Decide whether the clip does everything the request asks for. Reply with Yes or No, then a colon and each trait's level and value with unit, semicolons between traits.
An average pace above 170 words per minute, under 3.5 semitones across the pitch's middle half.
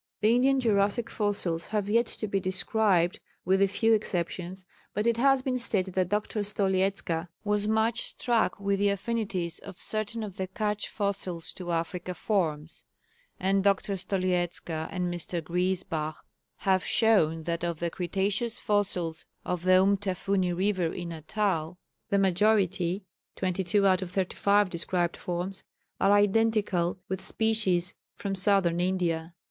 No: average, 140 wpm; average, 2.9 semitones